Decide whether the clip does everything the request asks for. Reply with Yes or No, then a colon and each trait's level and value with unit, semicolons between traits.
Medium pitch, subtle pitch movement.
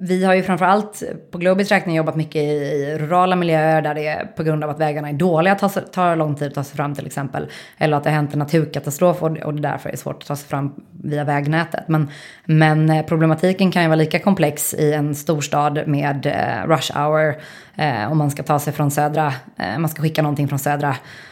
Yes: medium, 155 Hz; narrow, 2.1 semitones